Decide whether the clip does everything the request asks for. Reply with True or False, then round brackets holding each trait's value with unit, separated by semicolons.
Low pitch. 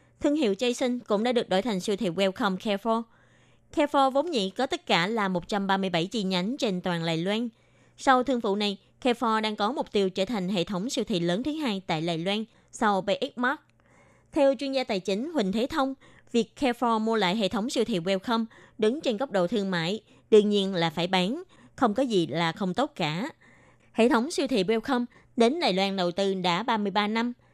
False (215 Hz)